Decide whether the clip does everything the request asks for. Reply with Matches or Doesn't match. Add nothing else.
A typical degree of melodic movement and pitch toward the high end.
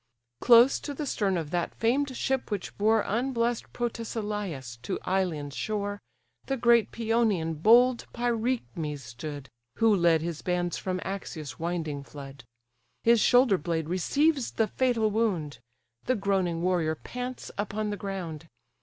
Doesn't match